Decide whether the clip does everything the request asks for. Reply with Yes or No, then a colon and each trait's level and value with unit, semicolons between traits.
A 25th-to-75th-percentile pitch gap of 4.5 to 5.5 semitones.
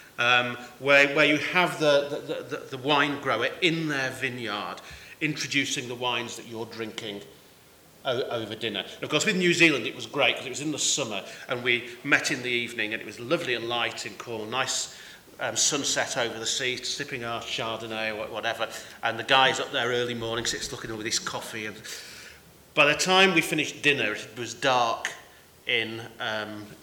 No: average, 3.8 semitones